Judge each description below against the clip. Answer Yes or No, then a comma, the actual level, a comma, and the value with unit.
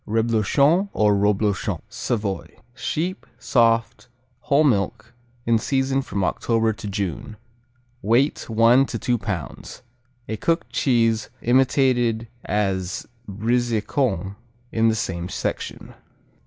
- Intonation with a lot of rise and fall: No, average, 3.5 semitones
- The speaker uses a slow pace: Yes, slow, 105 wpm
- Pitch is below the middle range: Yes, low, 115 Hz